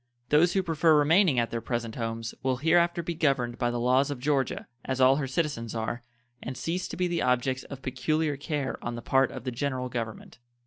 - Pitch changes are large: No, average, 4.2 semitones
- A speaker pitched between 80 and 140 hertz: Yes, low, 135 Hz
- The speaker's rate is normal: No, fast, 215 wpm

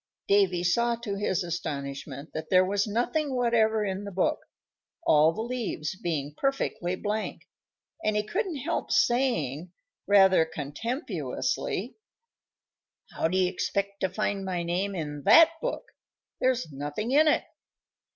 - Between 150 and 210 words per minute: No, slow, 135 wpm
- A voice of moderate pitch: No, high, 195 Hz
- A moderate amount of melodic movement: No, wide, 5.8 semitones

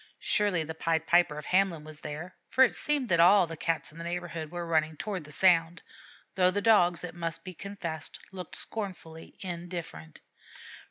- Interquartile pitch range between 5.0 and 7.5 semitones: No, narrow, 2.5 semitones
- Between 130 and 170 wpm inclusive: No, average, 180 wpm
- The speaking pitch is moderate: Yes, medium, 170 Hz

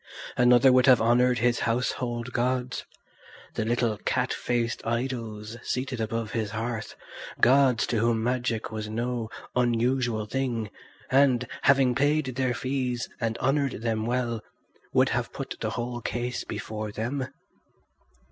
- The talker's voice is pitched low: Yes, low, 120 Hz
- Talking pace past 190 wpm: No, slow, 135 wpm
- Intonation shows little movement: Yes, narrow, 1.9 semitones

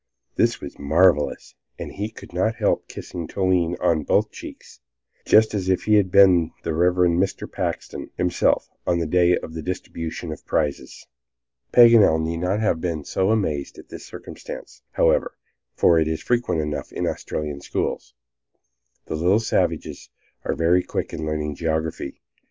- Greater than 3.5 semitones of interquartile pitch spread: No, average, 2.9 semitones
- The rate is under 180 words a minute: Yes, average, 160 wpm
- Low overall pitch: Yes, very low, 85 Hz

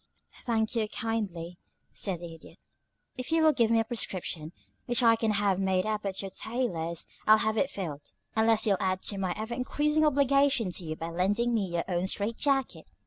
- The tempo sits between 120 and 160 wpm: No, average, 195 wpm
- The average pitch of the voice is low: No, high, 215 Hz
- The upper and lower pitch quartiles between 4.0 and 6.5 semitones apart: Yes, average, 4.4 semitones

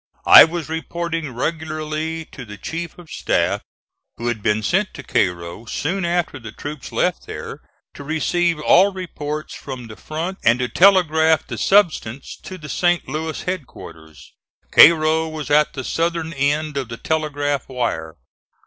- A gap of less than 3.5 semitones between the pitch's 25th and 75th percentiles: No, average, 4.3 semitones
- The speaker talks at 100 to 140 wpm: No, average, 155 wpm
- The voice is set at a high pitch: No, medium, 155 Hz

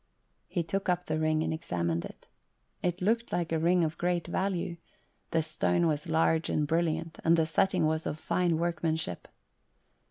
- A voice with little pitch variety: Yes, narrow, 1.8 semitones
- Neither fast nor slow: Yes, average, 170 wpm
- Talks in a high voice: No, medium, 165 Hz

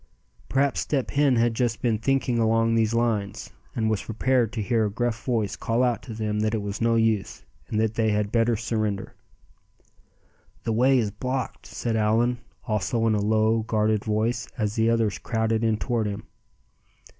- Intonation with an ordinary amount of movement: No, narrow, 1.7 semitones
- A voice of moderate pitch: No, low, 115 Hz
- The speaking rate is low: No, average, 180 wpm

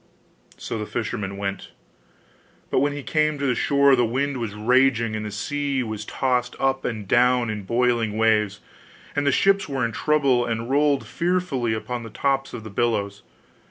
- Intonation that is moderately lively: Yes, average, 4.1 semitones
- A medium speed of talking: Yes, average, 180 wpm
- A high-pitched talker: No, low, 125 Hz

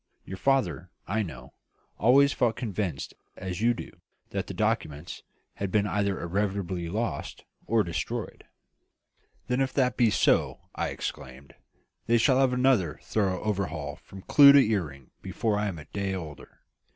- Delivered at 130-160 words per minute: Yes, average, 150 wpm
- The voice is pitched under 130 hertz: Yes, low, 100 Hz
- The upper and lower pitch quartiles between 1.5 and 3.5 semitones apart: No, average, 5.3 semitones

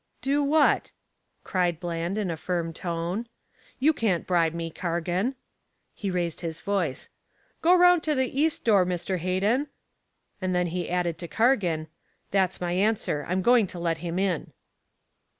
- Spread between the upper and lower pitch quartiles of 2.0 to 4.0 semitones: No, average, 4.6 semitones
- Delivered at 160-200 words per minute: No, average, 150 wpm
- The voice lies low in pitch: No, medium, 180 Hz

